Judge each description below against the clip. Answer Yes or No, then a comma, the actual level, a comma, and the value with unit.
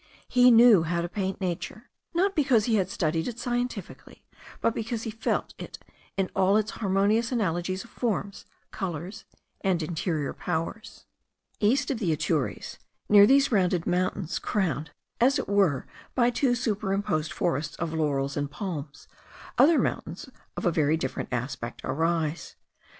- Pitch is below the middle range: No, high, 190 Hz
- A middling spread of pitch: No, wide, 5.8 semitones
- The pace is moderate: Yes, average, 150 wpm